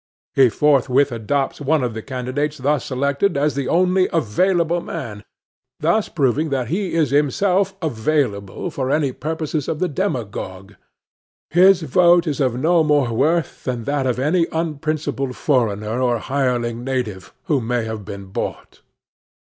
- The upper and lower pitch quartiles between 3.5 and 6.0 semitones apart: Yes, average, 4.7 semitones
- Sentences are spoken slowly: No, average, 150 wpm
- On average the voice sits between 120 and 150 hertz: Yes, medium, 140 Hz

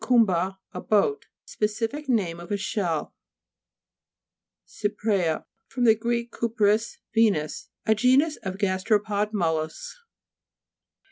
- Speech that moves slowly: Yes, slow, 95 wpm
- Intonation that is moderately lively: Yes, average, 3.4 semitones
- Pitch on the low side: No, high, 210 Hz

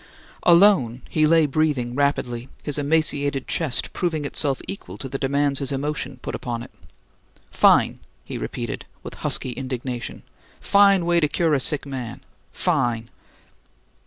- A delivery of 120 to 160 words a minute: Yes, average, 140 wpm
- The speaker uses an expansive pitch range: No, average, 3.7 semitones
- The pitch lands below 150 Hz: Yes, medium, 140 Hz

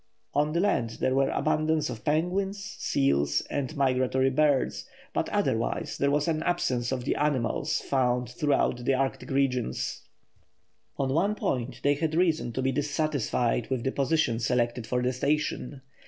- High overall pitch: No, low, 135 Hz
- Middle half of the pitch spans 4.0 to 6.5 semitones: No, average, 3.6 semitones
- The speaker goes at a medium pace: Yes, average, 155 wpm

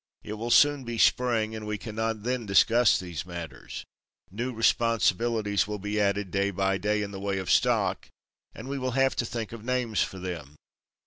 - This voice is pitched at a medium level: No, low, 110 Hz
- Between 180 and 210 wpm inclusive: Yes, average, 190 wpm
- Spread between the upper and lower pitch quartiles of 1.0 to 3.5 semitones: Yes, average, 3.1 semitones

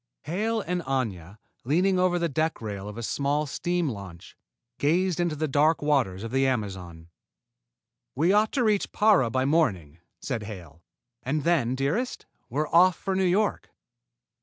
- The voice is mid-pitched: Yes, medium, 145 Hz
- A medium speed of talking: Yes, average, 160 wpm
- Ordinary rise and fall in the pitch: No, wide, 8.0 semitones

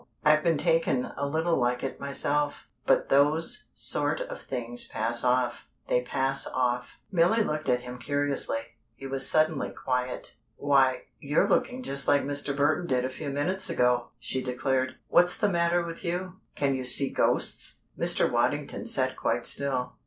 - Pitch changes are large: No, average, 4.4 semitones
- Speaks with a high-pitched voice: No, medium, 140 Hz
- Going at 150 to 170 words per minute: Yes, average, 165 wpm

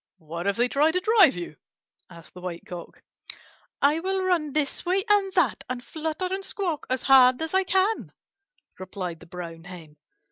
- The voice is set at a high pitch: Yes, very high, 280 Hz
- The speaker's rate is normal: Yes, average, 180 wpm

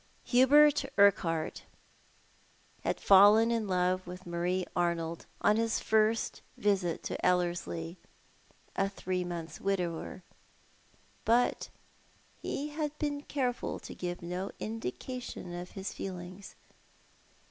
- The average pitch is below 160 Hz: No, high, 190 Hz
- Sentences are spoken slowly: Yes, slow, 105 wpm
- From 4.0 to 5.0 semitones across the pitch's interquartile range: Yes, average, 4.4 semitones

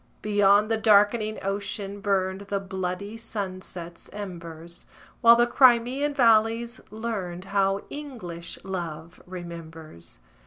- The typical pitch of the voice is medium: No, high, 200 Hz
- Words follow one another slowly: Yes, slow, 105 wpm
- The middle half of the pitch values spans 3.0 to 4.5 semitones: Yes, average, 3.8 semitones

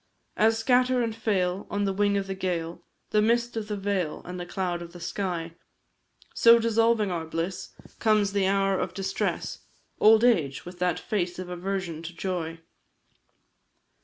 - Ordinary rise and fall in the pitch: Yes, average, 3.4 semitones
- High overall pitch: Yes, high, 195 Hz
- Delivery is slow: No, average, 165 wpm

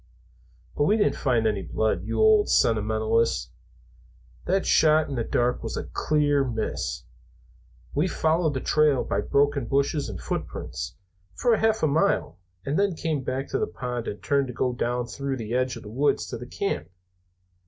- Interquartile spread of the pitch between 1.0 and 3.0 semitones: No, average, 4.7 semitones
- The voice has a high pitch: No, low, 135 Hz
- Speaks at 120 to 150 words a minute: No, average, 175 wpm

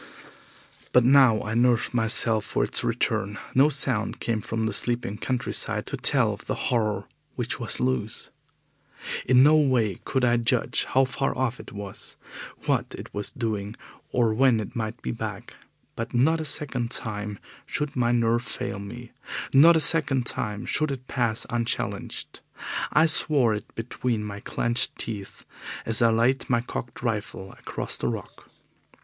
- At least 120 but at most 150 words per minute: No, average, 160 wpm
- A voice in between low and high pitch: No, low, 120 Hz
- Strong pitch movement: No, average, 3.0 semitones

